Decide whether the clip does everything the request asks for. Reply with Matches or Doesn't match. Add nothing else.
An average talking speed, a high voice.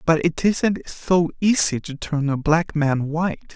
Doesn't match